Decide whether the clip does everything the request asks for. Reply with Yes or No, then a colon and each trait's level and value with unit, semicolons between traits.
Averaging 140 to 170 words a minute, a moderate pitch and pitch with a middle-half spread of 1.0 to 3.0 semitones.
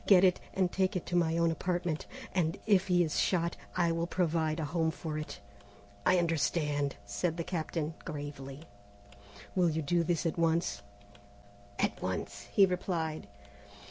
Yes: average, 160 wpm; medium, 165 Hz; narrow, 2.4 semitones